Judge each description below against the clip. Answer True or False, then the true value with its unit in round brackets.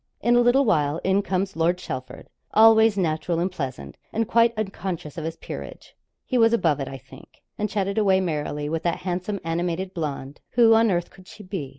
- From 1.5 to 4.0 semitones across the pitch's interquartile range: False (4.9 semitones)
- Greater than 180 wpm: True (200 wpm)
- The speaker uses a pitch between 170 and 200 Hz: True (185 Hz)